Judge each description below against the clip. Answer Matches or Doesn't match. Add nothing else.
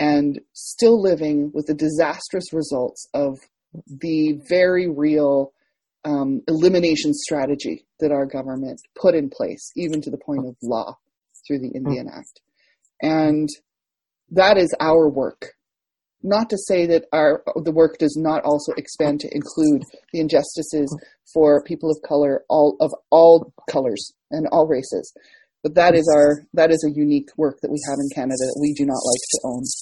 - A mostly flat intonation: Matches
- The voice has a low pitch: Doesn't match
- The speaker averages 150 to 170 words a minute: Matches